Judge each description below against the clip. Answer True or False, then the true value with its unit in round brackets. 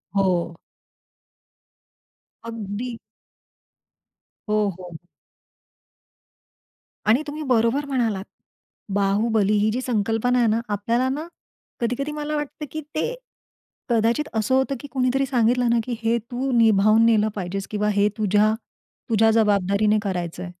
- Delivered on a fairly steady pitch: False (3.5 semitones)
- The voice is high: True (225 Hz)